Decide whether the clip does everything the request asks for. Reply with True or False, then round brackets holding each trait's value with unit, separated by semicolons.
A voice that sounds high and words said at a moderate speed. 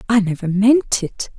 True (210 Hz; 175 wpm)